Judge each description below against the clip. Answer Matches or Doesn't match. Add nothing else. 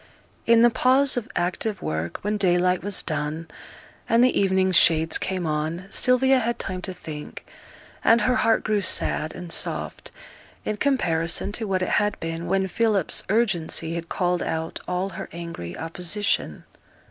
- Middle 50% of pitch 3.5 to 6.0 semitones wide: Matches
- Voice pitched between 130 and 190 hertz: Matches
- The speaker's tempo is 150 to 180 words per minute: Matches